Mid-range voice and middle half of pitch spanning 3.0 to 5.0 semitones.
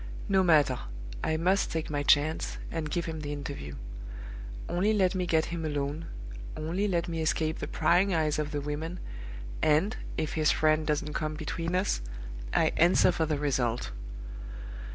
No: medium, 160 Hz; narrow, 2.6 semitones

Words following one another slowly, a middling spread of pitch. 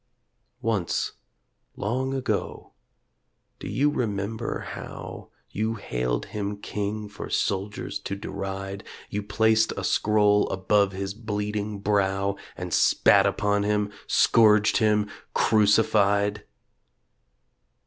No: slow, 100 wpm; narrow, 1.4 semitones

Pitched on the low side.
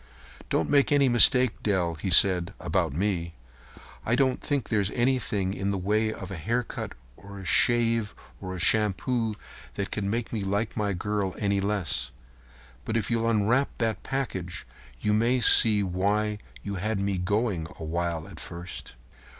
Yes: low, 105 Hz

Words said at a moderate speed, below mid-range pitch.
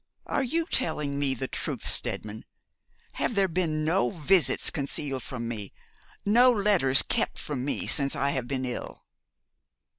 No: average, 150 wpm; medium, 145 Hz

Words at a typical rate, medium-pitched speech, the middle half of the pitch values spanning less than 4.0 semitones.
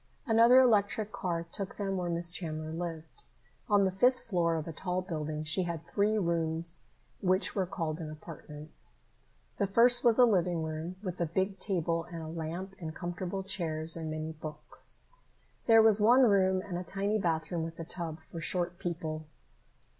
Yes: average, 175 wpm; medium, 175 Hz; average, 3.4 semitones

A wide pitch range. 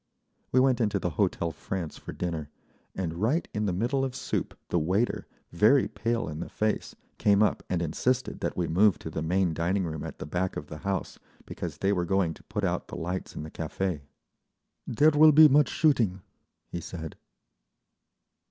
Yes: wide, 5.7 semitones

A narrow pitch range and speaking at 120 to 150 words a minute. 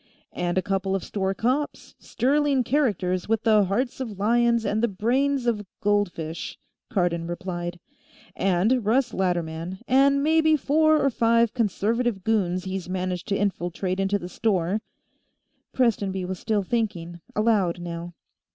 No: average, 4.6 semitones; average, 140 wpm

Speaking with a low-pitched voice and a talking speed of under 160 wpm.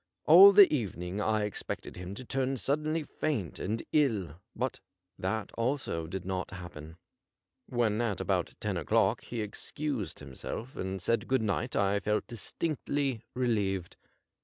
Yes: low, 110 Hz; average, 145 wpm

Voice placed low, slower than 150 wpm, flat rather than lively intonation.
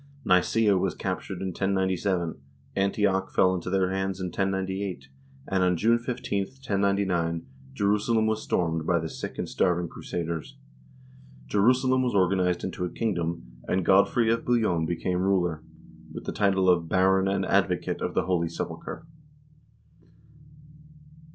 Yes: very low, 95 Hz; average, 140 wpm; narrow, 2.3 semitones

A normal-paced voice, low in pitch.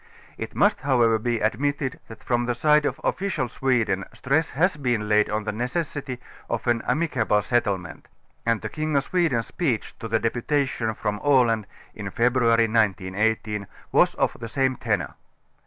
Yes: average, 165 wpm; low, 120 Hz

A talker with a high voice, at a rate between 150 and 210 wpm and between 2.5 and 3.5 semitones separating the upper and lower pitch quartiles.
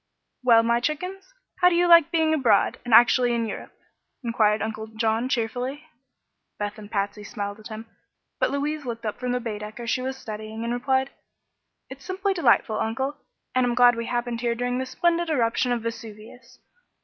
Yes: high, 240 Hz; average, 180 wpm; average, 3.2 semitones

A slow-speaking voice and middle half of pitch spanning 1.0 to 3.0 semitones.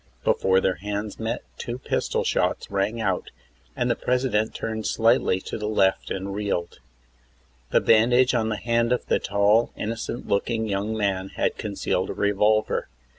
No: average, 160 wpm; narrow, 2.5 semitones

